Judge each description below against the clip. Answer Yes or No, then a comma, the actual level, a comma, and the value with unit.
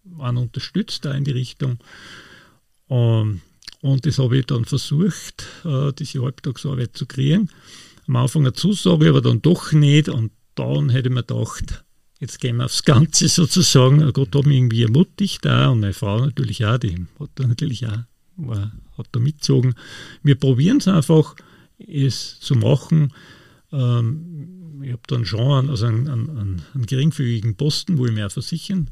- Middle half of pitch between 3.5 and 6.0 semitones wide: Yes, average, 3.8 semitones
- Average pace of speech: Yes, average, 160 wpm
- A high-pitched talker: No, low, 135 Hz